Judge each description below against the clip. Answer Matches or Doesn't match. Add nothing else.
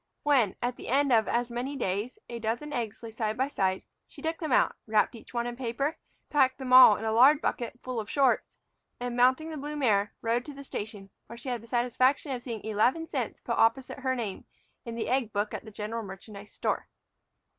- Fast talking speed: Matches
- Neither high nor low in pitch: Doesn't match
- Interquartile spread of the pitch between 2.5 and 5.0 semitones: Matches